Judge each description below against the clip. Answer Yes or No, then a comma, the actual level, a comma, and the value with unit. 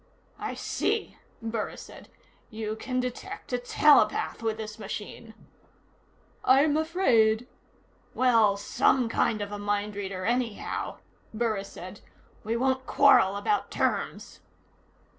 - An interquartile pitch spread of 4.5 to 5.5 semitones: No, average, 3.5 semitones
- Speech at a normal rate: No, slow, 120 wpm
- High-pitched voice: Yes, high, 225 Hz